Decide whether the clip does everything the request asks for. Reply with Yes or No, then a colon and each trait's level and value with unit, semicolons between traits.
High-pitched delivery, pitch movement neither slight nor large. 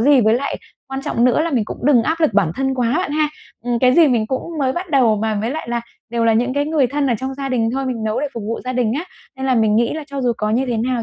Yes: very high, 255 Hz; average, 3.4 semitones